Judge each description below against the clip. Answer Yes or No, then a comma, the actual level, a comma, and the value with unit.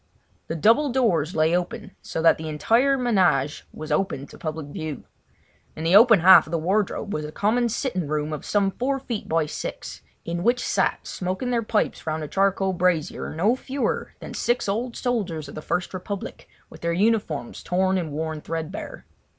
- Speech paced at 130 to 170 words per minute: No, average, 185 wpm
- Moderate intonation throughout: No, wide, 6.1 semitones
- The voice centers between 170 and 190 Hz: Yes, medium, 185 Hz